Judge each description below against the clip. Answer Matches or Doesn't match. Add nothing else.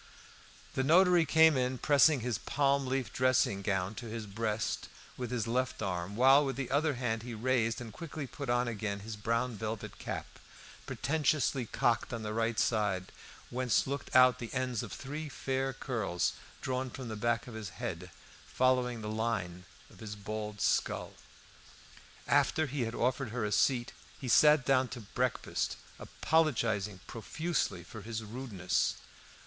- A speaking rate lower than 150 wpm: Doesn't match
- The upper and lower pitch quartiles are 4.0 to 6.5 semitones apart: Doesn't match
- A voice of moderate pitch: Doesn't match